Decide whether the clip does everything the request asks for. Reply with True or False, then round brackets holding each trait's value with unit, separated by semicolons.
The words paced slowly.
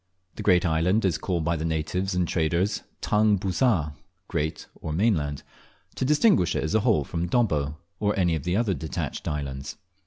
False (175 wpm)